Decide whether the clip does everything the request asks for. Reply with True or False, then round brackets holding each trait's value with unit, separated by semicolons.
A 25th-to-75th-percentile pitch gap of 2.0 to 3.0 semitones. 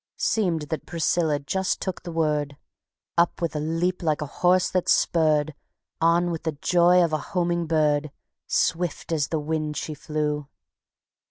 True (2.4 semitones)